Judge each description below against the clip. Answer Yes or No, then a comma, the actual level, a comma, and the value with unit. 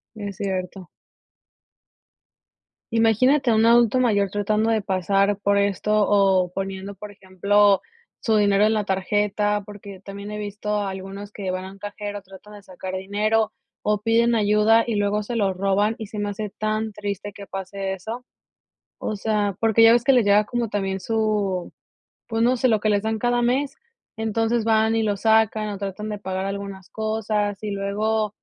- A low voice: No, high, 205 Hz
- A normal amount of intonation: No, narrow, 1.9 semitones